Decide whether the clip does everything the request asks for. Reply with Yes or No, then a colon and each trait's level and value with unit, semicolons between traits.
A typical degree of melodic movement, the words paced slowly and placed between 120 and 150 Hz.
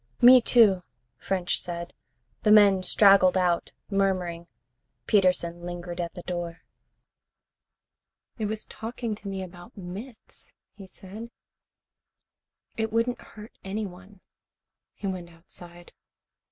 No: average, 3.2 semitones; slow, 110 wpm; high, 190 Hz